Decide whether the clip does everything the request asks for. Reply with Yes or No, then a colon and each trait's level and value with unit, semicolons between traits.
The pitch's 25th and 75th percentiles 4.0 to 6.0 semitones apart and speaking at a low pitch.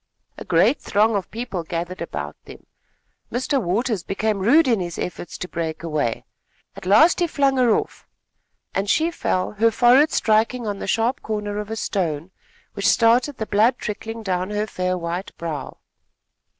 No: average, 4.7 semitones; high, 210 Hz